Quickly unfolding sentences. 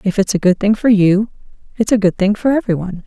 Yes: fast, 255 wpm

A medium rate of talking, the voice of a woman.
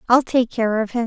No: fast, 280 wpm; female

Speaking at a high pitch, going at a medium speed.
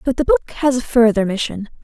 No: high, 225 Hz; fast, 230 wpm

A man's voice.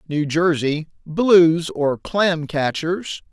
Yes: male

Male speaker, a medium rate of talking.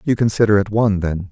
No: male; fast, 230 wpm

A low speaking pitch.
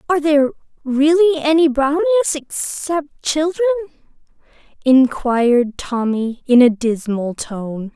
No: very high, 285 Hz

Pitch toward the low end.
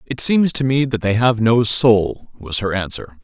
Yes: low, 115 Hz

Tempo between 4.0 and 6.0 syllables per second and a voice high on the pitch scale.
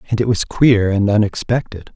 No: 5.2 syllables/s; low, 105 Hz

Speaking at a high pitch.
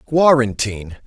No: low, 125 Hz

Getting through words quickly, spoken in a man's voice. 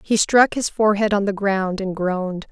No: fast, 215 wpm; female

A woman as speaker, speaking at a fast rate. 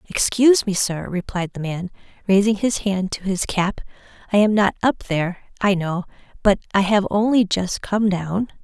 No: female; average, 180 wpm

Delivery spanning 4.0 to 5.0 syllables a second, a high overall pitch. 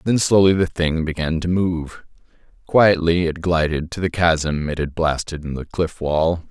No: 4.4 syllables/s; very low, 85 Hz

